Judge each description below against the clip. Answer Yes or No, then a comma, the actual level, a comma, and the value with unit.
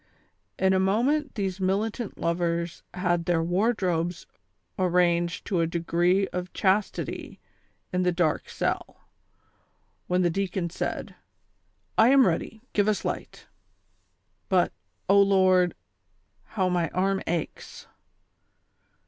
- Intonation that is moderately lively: No, narrow, 2.3 semitones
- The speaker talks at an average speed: No, slow, 115 wpm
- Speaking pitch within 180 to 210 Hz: Yes, medium, 185 Hz